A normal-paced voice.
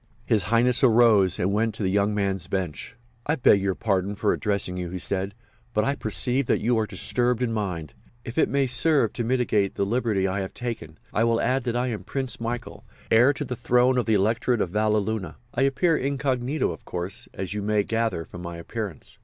No: fast, 210 wpm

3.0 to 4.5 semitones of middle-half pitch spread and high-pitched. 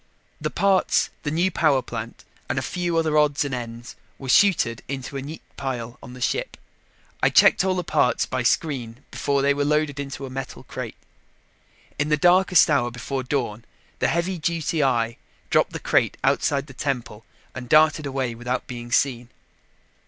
No: average, 3.9 semitones; medium, 140 Hz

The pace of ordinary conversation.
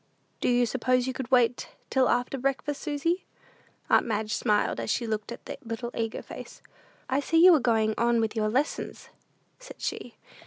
Yes: average, 185 wpm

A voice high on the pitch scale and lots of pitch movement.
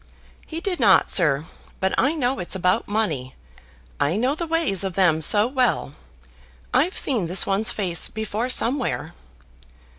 Yes: high, 210 Hz; wide, 6.2 semitones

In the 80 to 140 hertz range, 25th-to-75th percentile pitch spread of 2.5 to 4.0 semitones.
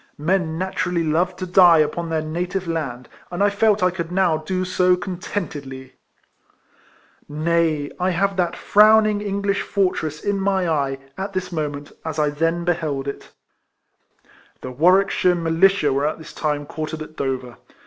No: medium, 170 Hz; average, 3.5 semitones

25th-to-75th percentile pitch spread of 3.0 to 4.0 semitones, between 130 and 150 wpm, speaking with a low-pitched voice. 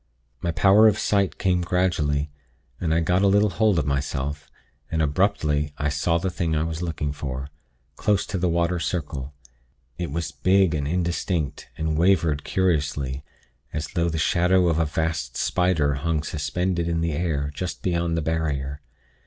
No: average, 3.3 semitones; average, 170 wpm; very low, 80 Hz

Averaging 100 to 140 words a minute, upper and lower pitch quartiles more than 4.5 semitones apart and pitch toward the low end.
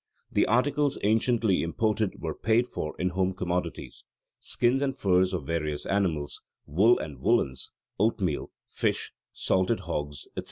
Yes: slow, 135 wpm; wide, 5.5 semitones; very low, 95 Hz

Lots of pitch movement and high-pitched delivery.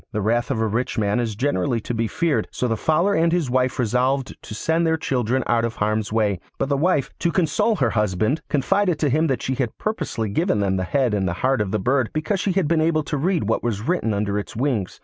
No: wide, 6.3 semitones; low, 125 Hz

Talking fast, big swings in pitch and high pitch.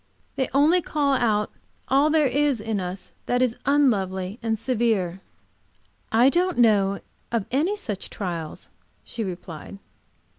No: slow, 135 wpm; wide, 6.0 semitones; high, 230 Hz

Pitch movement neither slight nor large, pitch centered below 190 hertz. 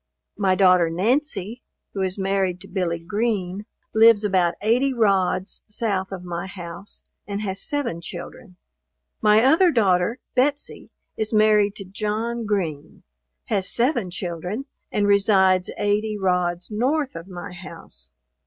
No: average, 3.3 semitones; high, 200 Hz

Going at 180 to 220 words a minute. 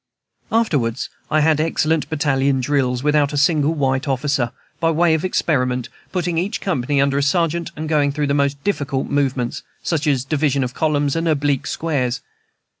No: average, 165 wpm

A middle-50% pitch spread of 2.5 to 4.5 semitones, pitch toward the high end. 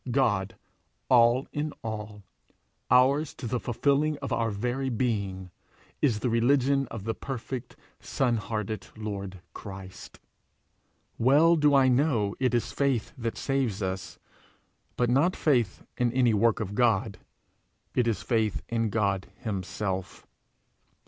No: average, 4.1 semitones; low, 115 Hz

